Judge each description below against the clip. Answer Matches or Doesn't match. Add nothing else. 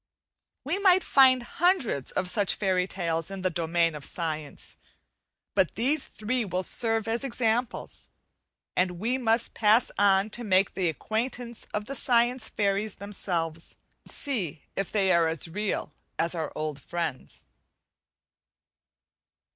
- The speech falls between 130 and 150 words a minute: Matches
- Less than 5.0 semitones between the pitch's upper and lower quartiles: Doesn't match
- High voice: Matches